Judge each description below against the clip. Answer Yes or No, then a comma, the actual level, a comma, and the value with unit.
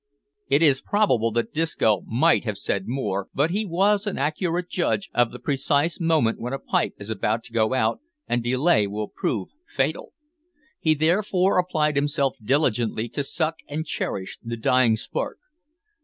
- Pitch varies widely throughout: Yes, wide, 6.4 semitones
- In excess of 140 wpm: Yes, average, 165 wpm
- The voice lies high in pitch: No, medium, 140 Hz